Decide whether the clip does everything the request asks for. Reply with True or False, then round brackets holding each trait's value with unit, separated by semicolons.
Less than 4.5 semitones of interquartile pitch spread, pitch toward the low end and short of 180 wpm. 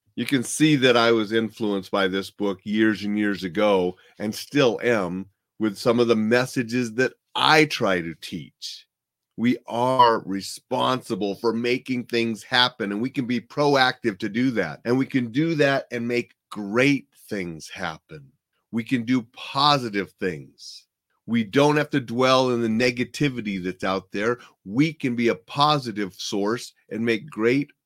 True (3.9 semitones; 120 Hz; 165 wpm)